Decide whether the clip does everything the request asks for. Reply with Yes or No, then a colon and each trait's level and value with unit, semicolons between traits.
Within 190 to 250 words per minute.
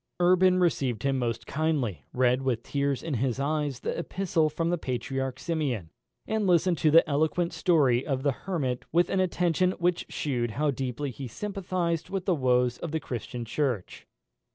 No: average, 175 wpm